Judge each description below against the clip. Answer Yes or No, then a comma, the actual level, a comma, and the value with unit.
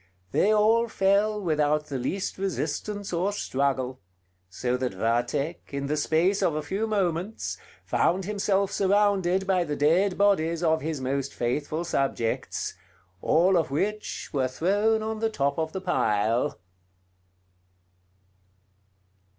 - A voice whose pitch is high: No, medium, 170 Hz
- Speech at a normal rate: No, slow, 130 wpm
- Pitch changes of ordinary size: No, wide, 6.1 semitones